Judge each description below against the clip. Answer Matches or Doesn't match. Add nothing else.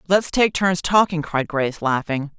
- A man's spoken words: Doesn't match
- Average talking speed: Matches